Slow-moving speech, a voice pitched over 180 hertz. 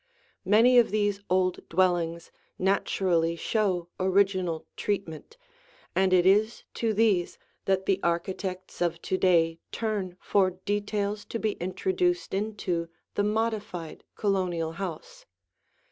Yes: slow, 115 wpm; high, 190 Hz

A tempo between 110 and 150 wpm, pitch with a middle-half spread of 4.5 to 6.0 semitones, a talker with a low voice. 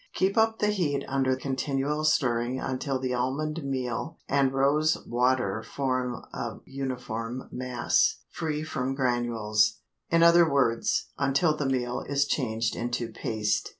No: slow, 135 wpm; average, 3.1 semitones; low, 130 Hz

